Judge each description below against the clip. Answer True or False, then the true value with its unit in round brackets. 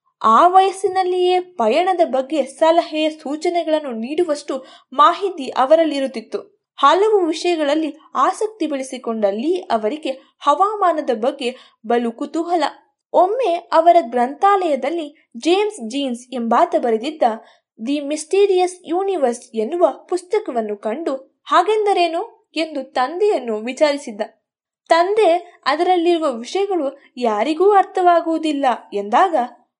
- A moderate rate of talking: True (85 wpm)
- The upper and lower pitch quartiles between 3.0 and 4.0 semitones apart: False (5.5 semitones)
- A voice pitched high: True (310 Hz)